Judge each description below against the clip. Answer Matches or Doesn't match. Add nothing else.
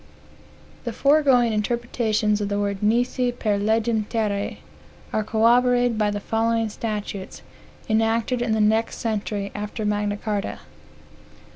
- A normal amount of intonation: Doesn't match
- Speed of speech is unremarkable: Doesn't match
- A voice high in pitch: Matches